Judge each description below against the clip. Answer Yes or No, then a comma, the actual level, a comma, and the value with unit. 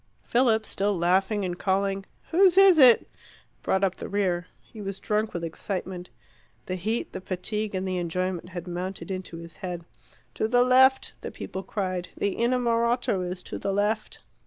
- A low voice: No, high, 195 Hz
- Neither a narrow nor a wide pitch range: Yes, average, 3.4 semitones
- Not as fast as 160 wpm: No, average, 170 wpm